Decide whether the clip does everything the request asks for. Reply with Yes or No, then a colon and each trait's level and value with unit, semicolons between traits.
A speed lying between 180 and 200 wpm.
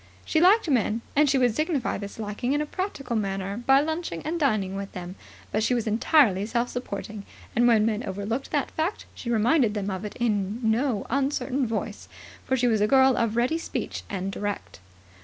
Yes: average, 195 wpm